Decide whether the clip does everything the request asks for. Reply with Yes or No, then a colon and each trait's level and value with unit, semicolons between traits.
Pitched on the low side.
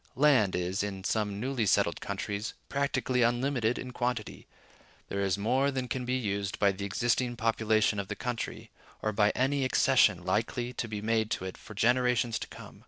Yes: low, 115 Hz